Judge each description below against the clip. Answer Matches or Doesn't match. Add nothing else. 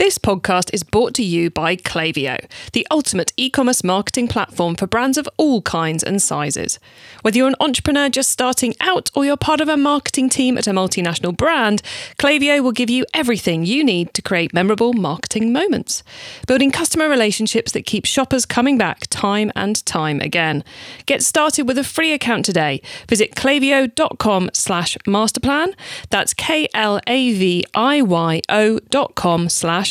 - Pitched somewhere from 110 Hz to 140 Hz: Doesn't match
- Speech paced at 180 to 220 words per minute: Doesn't match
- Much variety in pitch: Matches